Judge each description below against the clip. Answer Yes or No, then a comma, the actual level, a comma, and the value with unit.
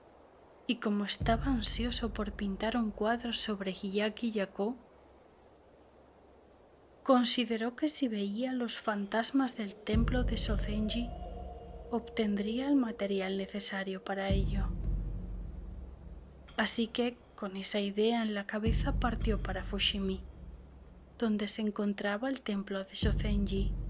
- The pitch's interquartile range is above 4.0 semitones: No, average, 3.2 semitones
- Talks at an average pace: No, slow, 115 wpm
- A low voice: No, high, 210 Hz